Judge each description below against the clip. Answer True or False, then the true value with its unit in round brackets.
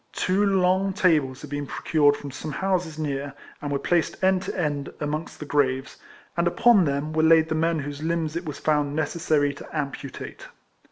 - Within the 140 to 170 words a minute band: False (185 wpm)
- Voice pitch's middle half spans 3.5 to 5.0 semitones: False (3.0 semitones)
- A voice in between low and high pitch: True (155 Hz)